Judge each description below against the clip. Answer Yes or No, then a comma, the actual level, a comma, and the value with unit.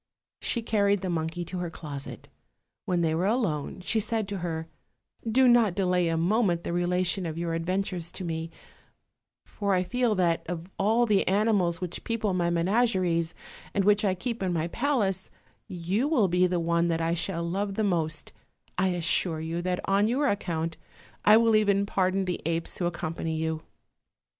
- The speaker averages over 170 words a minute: Yes, average, 180 wpm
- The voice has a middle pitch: Yes, medium, 180 Hz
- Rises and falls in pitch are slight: No, average, 3.4 semitones